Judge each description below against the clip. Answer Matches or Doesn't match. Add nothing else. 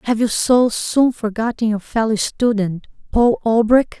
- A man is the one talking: Doesn't match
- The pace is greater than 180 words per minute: Doesn't match